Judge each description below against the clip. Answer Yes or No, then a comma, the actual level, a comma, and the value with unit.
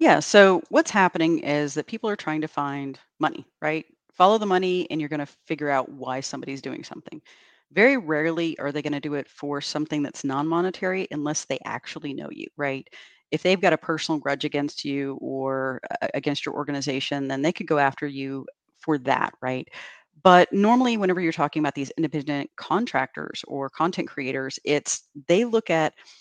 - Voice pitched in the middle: Yes, medium, 150 Hz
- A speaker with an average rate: Yes, average, 190 wpm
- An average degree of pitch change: Yes, average, 3.9 semitones